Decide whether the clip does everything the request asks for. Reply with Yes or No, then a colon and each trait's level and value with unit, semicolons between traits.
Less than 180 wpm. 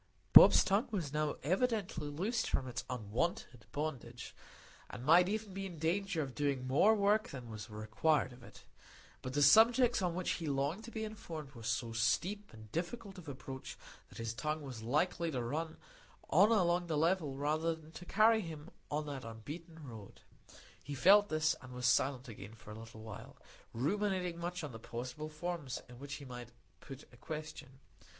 No: average, 185 wpm